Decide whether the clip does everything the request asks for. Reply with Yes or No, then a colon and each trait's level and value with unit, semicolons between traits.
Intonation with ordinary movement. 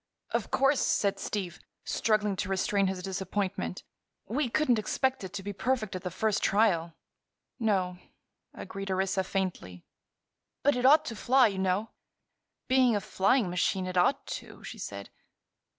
Yes: average, 4.1 semitones